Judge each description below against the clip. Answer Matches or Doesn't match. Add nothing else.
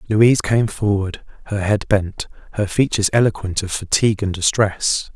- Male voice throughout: Matches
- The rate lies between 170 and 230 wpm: Doesn't match